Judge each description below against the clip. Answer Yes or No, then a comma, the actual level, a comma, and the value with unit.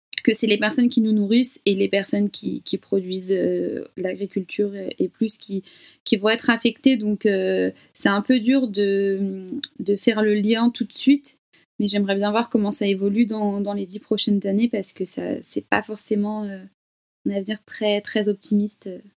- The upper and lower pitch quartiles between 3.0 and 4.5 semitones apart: No, narrow, 2.4 semitones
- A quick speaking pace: No, average, 190 wpm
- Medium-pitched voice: No, high, 210 Hz